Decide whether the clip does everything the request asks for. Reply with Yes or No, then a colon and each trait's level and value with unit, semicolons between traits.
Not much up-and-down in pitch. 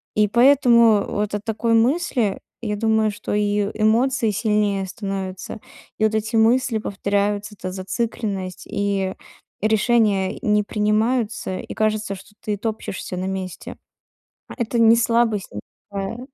Yes: narrow, 2.3 semitones